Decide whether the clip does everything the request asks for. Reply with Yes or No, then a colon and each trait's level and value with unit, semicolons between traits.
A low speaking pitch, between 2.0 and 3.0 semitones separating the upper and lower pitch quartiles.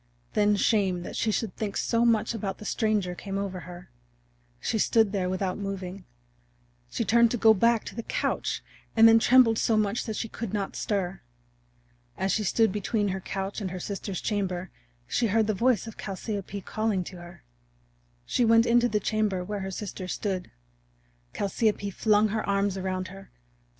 No: high, 205 Hz; narrow, 2.6 semitones